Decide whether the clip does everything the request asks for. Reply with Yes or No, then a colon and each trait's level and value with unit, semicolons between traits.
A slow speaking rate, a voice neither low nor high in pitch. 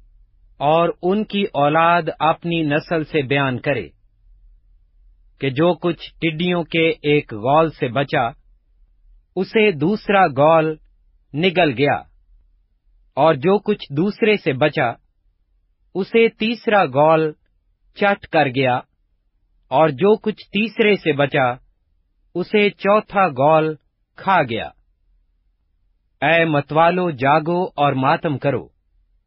Yes: slow, 105 wpm; medium, 150 Hz